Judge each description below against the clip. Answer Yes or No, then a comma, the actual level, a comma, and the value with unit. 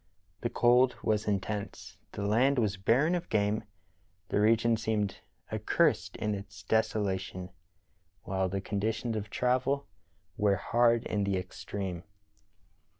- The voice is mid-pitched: No, low, 105 Hz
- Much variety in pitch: No, average, 3.0 semitones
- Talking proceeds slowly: Yes, slow, 125 wpm